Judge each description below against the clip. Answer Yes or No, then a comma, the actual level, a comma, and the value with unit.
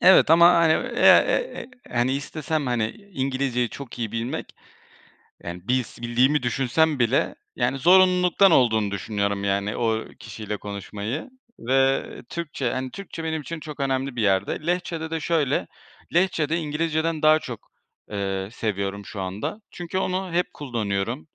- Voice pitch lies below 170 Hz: Yes, low, 135 Hz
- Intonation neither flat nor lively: No, wide, 6.5 semitones